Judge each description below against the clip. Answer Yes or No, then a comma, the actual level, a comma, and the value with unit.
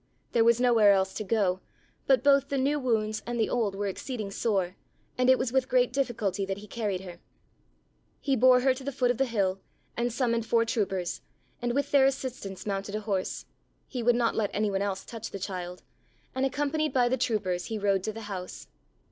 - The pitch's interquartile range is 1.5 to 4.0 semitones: No, average, 4.4 semitones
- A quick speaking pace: Yes, fast, 210 wpm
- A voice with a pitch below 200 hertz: No, high, 225 Hz